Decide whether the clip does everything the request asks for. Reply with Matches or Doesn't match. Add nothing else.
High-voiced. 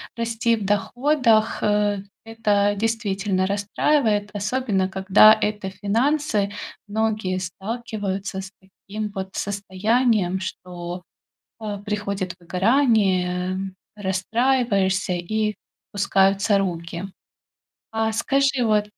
Matches